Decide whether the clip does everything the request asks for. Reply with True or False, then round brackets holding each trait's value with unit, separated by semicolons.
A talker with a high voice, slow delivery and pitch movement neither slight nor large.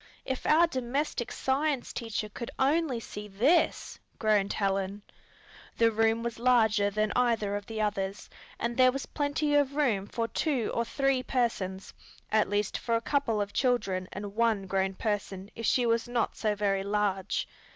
False (225 Hz; 165 wpm; 3.7 semitones)